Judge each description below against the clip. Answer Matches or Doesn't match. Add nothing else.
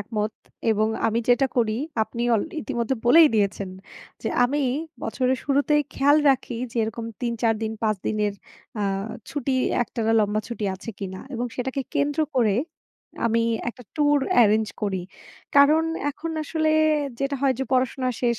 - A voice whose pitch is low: Doesn't match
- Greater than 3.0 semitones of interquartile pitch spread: Matches